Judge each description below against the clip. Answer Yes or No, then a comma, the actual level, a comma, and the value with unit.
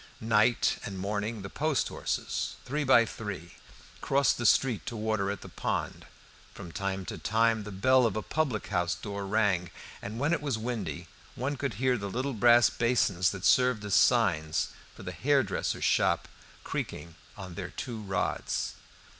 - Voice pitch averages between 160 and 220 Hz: No, low, 110 Hz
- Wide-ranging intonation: No, average, 4.1 semitones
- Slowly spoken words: No, average, 170 wpm